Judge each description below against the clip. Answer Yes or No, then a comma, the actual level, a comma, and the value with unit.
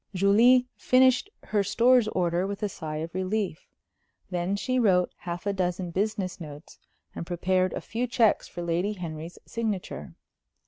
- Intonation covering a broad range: No, average, 3.8 semitones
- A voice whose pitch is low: No, high, 190 Hz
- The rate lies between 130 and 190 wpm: Yes, average, 150 wpm